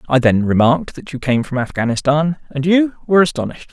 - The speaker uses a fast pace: No, average, 195 wpm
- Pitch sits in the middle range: Yes, medium, 145 Hz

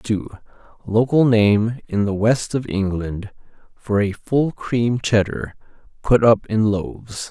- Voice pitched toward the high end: No, low, 110 Hz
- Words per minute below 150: Yes, average, 140 wpm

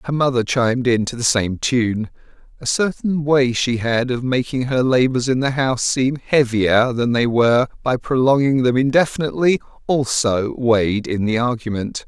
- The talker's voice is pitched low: Yes, low, 125 Hz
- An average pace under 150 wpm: No, average, 170 wpm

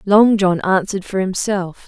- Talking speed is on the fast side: No, average, 160 wpm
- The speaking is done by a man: No, female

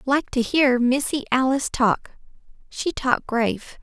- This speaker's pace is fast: No, average, 140 wpm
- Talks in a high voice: Yes, very high, 260 Hz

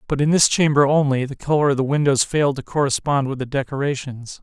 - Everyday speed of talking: No, fast, 215 wpm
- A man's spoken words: Yes, male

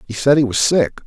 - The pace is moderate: No, fast, 285 wpm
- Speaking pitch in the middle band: No, low, 125 Hz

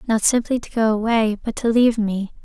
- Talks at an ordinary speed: No, fast, 220 wpm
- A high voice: Yes, high, 225 Hz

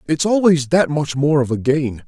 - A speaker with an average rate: No, fast, 230 wpm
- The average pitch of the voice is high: No, medium, 150 Hz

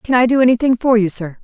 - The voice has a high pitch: Yes, high, 235 Hz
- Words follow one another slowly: No, fast, 295 wpm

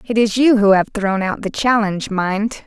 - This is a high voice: Yes, high, 210 Hz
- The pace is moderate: No, fast, 225 wpm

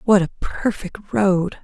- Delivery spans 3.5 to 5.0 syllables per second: Yes, 4.1 syllables/s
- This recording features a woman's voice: Yes, female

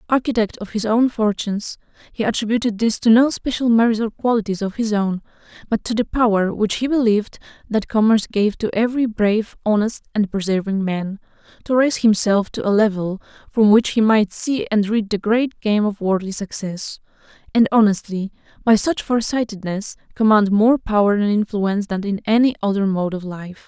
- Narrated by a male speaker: No, female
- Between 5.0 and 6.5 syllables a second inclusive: Yes, 5.4 syllables/s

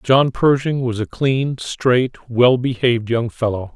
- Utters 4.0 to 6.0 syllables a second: No, 3.8 syllables/s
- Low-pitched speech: Yes, low, 125 Hz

